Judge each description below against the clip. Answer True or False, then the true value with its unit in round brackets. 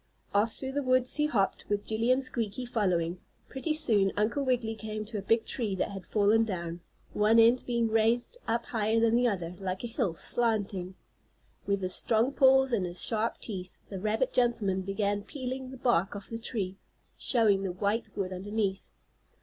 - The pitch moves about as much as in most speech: True (3.5 semitones)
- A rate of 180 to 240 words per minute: True (185 wpm)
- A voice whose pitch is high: True (220 Hz)